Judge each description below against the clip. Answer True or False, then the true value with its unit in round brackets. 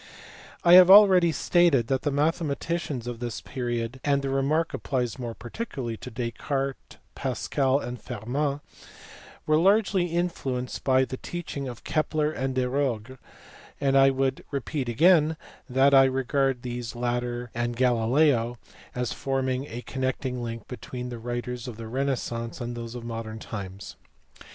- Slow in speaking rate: False (145 wpm)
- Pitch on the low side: True (130 Hz)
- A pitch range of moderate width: True (3.0 semitones)